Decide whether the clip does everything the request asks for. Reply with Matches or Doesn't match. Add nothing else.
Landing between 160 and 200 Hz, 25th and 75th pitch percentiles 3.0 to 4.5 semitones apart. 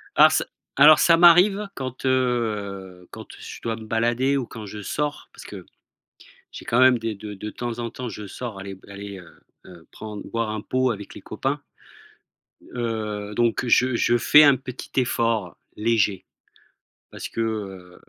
Doesn't match